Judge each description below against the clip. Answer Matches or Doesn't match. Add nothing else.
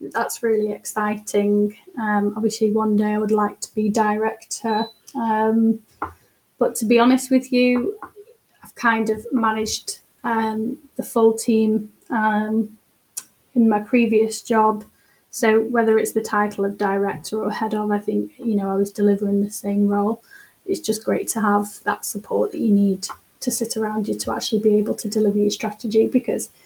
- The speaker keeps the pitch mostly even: Matches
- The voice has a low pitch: Doesn't match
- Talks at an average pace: Matches